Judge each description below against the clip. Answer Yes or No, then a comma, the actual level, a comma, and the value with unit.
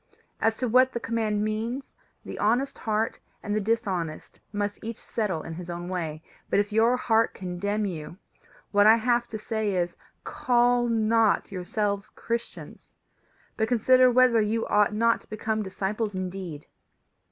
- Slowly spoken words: No, average, 155 wpm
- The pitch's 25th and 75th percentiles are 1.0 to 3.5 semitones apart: Yes, average, 3.0 semitones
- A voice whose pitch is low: No, high, 215 Hz